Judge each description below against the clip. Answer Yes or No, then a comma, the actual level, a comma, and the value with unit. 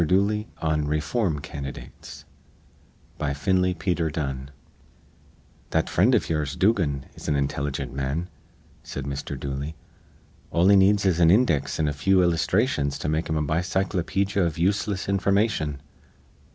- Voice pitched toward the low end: Yes, very low, 80 Hz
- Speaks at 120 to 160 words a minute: Yes, average, 140 wpm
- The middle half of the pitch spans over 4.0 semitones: Yes, average, 4.8 semitones